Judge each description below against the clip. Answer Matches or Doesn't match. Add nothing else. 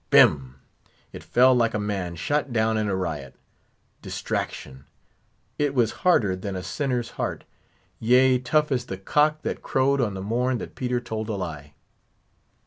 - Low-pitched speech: Matches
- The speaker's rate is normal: Matches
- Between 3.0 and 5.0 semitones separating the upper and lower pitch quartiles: Doesn't match